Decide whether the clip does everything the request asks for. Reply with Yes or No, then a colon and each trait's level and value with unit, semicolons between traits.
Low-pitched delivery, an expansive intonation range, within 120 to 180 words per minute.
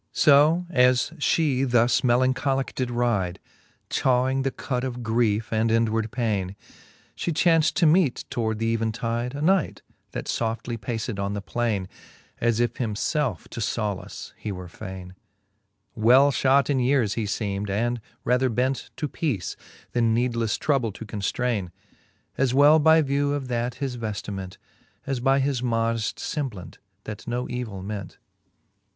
No: low, 120 Hz; average, 3.5 semitones; average, 145 wpm